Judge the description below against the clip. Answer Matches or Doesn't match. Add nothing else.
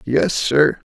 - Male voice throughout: Matches